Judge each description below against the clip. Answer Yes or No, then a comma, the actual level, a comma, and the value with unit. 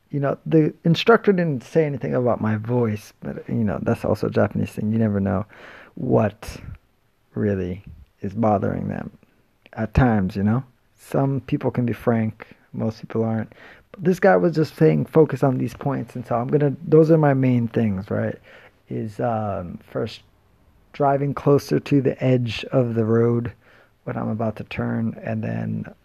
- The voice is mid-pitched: No, low, 120 Hz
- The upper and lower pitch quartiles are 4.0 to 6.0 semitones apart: Yes, average, 4.4 semitones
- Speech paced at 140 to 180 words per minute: Yes, average, 175 wpm